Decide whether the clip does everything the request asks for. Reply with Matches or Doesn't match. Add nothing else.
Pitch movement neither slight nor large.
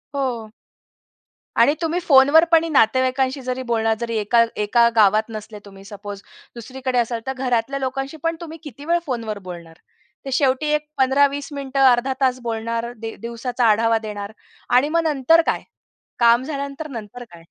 Matches